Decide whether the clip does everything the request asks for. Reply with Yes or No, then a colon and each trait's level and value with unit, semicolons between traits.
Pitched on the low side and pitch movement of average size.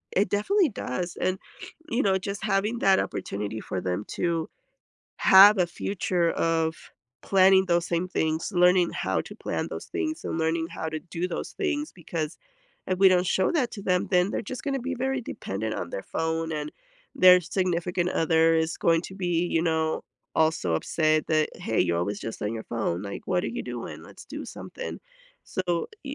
No: medium, 175 Hz; average, 3.1 semitones